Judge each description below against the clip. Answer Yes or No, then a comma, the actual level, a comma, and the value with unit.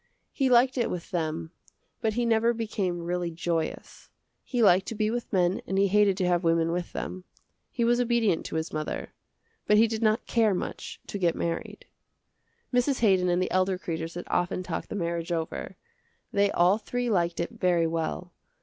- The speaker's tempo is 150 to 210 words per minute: Yes, average, 190 wpm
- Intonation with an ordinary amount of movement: Yes, average, 4.5 semitones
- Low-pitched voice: No, medium, 185 Hz